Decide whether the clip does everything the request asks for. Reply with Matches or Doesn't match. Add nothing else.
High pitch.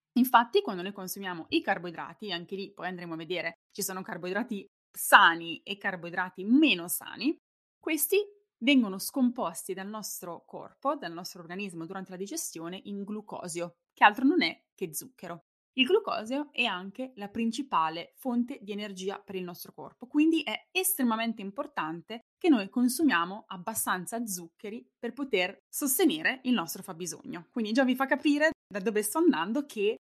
Matches